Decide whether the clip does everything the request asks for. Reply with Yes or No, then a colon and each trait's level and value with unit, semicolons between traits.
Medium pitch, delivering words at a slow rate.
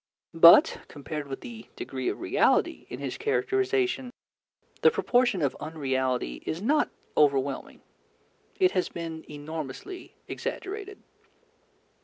Yes: medium, 160 Hz; slow, 110 wpm